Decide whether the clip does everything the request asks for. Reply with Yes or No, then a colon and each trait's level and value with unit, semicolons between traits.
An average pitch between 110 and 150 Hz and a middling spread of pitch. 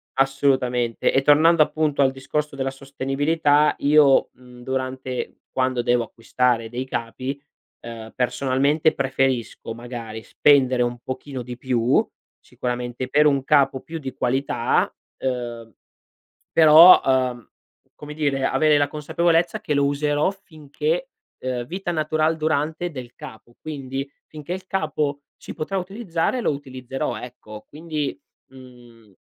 Yes: low, 135 Hz; average, 3.4 semitones